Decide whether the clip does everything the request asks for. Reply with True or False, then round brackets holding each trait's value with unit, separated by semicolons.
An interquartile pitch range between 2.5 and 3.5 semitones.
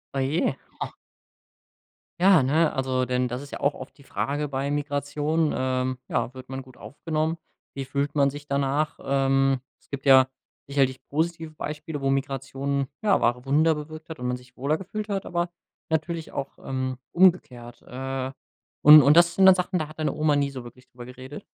True (2.9 semitones)